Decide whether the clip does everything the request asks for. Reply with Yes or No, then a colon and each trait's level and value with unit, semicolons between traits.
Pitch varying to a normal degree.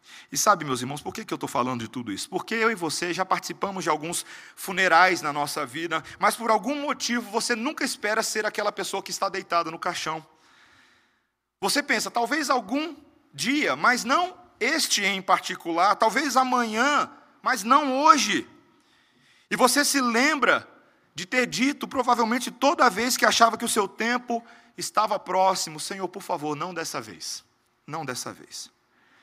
No: wide, 6.4 semitones